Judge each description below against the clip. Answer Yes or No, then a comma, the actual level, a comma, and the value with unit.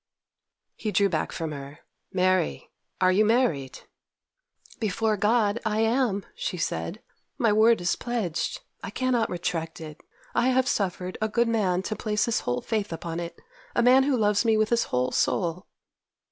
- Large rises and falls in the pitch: No, average, 4.9 semitones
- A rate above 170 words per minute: No, average, 160 wpm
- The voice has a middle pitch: No, high, 210 Hz